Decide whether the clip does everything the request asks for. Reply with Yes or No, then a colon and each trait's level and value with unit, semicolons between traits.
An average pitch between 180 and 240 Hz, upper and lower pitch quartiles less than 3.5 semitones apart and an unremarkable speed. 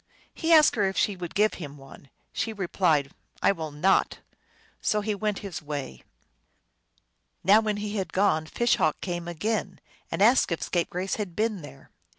No: high, 190 Hz; average, 4.8 semitones; average, 175 wpm